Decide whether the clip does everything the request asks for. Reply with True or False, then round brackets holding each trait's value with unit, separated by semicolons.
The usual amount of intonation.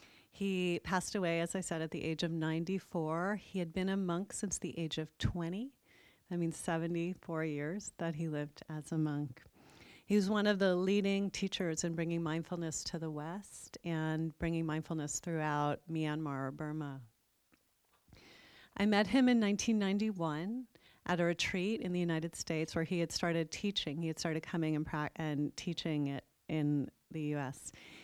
True (3.2 semitones)